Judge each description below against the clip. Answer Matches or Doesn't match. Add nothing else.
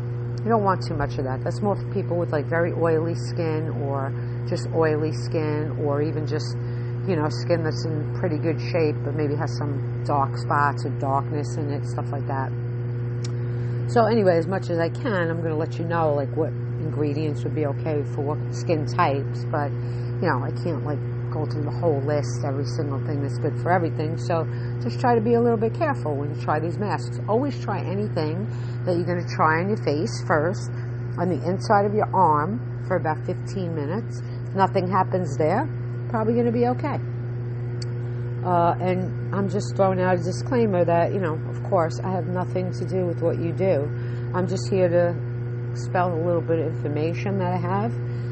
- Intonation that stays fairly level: Matches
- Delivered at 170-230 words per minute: Matches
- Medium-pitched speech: Doesn't match